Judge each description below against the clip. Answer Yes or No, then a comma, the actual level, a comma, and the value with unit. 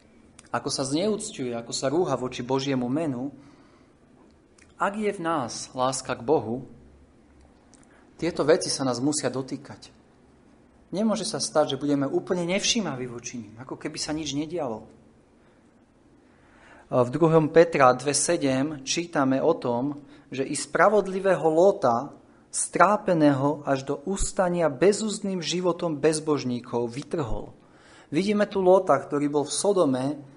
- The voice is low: No, medium, 145 Hz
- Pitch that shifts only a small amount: No, average, 4.7 semitones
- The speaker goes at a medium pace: Yes, average, 125 wpm